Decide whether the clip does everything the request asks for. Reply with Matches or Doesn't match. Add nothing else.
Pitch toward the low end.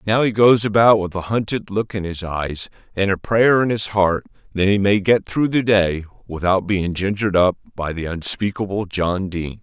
Matches